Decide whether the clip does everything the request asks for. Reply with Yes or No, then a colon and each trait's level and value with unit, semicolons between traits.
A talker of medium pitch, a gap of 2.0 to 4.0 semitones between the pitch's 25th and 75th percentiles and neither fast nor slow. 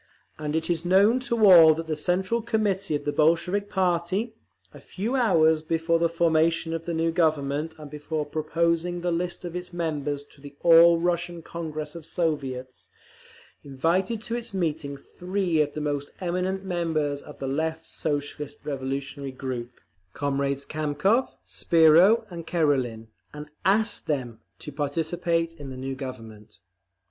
Yes: medium, 160 Hz; average, 3.4 semitones; average, 155 wpm